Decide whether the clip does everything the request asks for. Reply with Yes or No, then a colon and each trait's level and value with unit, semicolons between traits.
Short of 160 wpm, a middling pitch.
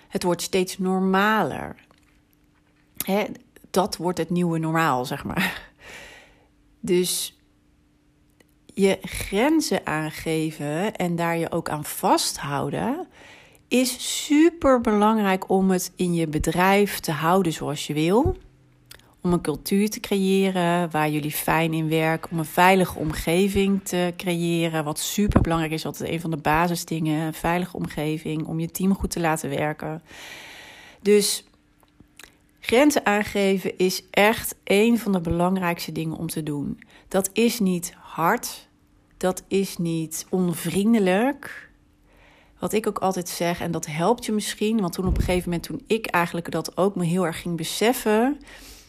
Yes: average, 140 wpm; medium, 180 Hz